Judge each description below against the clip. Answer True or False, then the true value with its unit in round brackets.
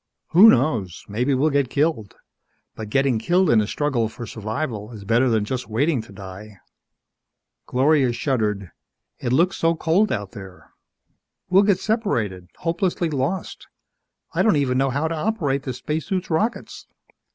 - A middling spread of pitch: False (6.7 semitones)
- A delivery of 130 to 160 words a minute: True (150 wpm)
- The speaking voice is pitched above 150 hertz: False (130 Hz)